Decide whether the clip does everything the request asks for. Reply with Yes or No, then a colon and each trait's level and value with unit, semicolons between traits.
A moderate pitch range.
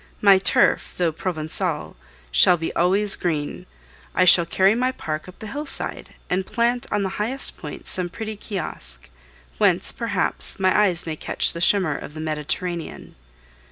Yes: average, 4.5 semitones